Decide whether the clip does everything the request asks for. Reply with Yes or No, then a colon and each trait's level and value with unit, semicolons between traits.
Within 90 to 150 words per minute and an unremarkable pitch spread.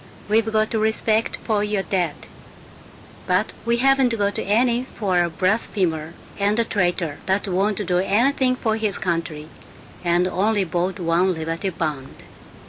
Yes: average, 140 wpm; average, 4.0 semitones